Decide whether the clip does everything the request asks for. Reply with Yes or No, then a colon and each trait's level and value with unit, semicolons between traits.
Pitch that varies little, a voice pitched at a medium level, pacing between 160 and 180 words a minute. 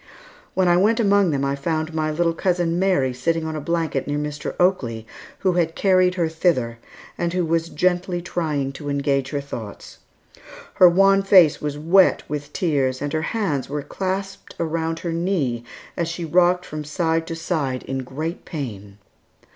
No: average, 3.8 semitones; medium, 165 Hz; average, 175 wpm